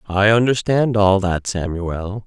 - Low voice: Yes, low, 100 Hz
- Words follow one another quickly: No, slow, 135 wpm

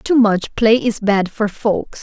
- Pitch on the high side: Yes, high, 215 Hz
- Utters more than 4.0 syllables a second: No, 3.5 syllables/s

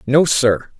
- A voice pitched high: No, low, 135 Hz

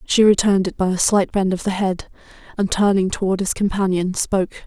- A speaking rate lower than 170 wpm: No, fast, 205 wpm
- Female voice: Yes, female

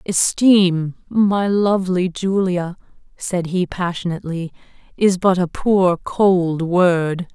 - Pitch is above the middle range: No, medium, 180 Hz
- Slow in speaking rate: Yes, slow, 105 wpm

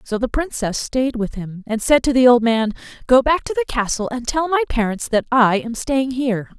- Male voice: No, female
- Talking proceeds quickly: Yes, fast, 235 wpm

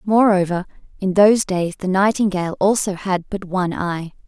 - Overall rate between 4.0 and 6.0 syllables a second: Yes, 5.2 syllables/s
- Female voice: Yes, female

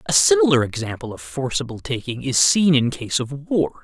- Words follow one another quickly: No, average, 190 wpm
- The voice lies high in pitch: No, medium, 140 Hz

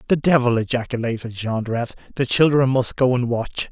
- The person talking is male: Yes, male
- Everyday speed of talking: Yes, average, 160 wpm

